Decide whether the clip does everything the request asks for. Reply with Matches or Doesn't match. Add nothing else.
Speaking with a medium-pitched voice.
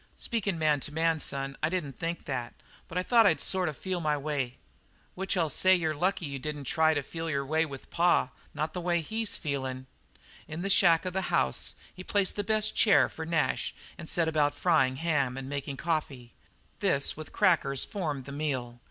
Matches